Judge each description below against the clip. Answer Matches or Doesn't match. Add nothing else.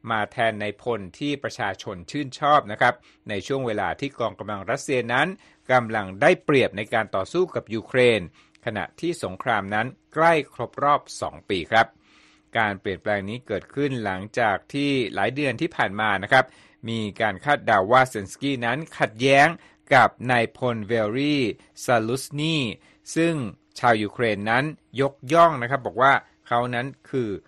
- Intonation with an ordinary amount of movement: Matches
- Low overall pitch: Matches